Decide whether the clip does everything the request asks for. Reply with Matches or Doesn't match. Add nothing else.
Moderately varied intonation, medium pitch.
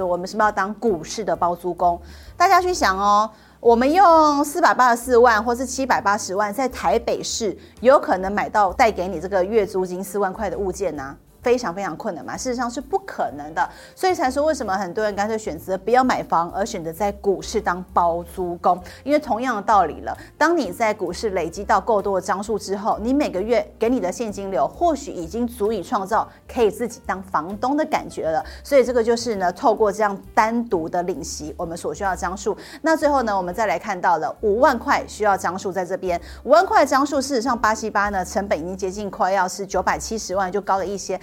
Doesn't match